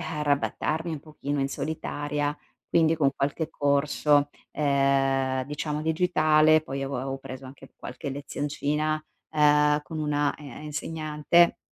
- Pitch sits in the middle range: Yes, medium, 150 Hz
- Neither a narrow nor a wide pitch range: No, narrow, 1.7 semitones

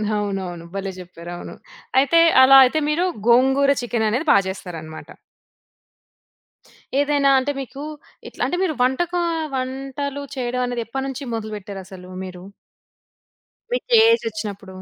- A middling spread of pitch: No, wide, 6.0 semitones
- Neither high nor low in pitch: No, high, 245 Hz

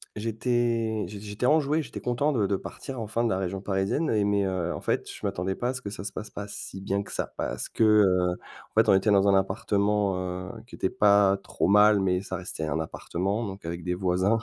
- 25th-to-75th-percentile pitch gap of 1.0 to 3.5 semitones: Yes, average, 2.7 semitones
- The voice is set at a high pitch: No, low, 100 Hz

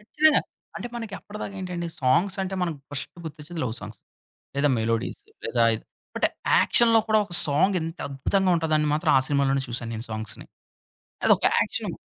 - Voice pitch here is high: No, medium, 155 Hz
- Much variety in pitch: Yes, wide, 6.2 semitones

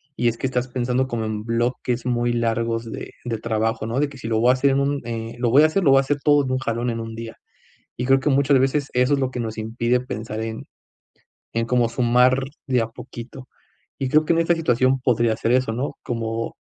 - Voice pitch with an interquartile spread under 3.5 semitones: Yes, narrow, 2.6 semitones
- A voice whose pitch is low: Yes, low, 125 Hz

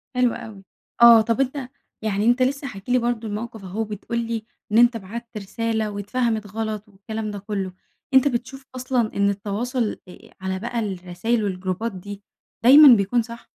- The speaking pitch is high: Yes, high, 220 Hz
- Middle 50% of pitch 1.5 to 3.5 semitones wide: Yes, average, 3.0 semitones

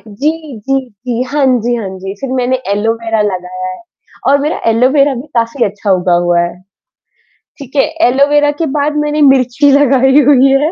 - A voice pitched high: Yes, very high, 255 Hz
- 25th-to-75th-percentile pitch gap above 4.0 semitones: Yes, average, 4.9 semitones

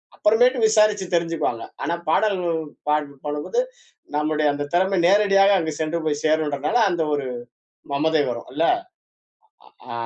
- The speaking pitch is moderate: Yes, medium, 160 Hz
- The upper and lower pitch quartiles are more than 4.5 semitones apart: Yes, average, 5.0 semitones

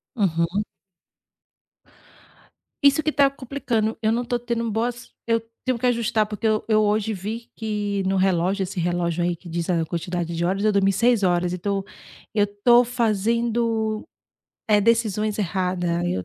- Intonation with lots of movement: No, average, 4.2 semitones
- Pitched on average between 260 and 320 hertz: No, high, 210 Hz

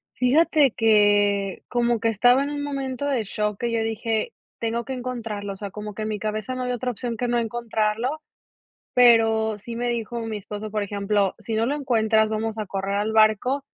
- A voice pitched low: No, high, 225 Hz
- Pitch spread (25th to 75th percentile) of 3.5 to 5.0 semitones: No, narrow, 2.6 semitones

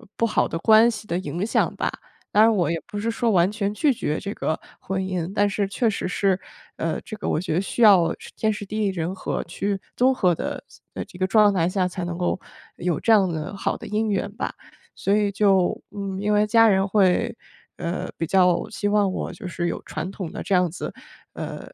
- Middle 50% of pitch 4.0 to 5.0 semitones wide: No, average, 2.7 semitones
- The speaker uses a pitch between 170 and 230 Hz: Yes, high, 195 Hz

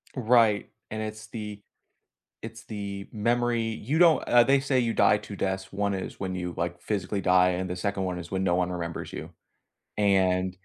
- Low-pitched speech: Yes, low, 100 Hz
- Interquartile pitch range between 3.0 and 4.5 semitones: Yes, average, 3.5 semitones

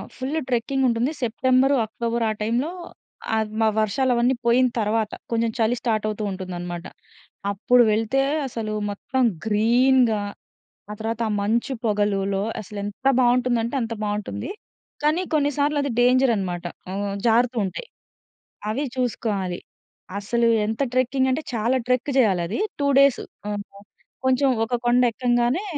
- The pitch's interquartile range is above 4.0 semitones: No, average, 3.4 semitones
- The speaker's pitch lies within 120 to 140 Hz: No, high, 235 Hz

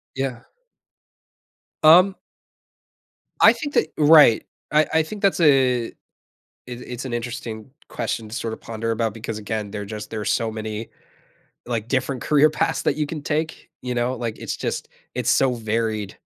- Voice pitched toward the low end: Yes, low, 120 Hz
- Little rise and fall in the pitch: No, average, 4.7 semitones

